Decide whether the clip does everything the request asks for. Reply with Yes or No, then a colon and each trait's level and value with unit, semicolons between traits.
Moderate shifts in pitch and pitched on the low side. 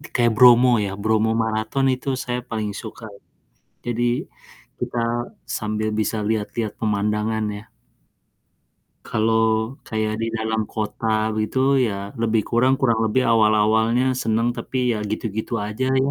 No: narrow, 1.6 semitones; low, 110 Hz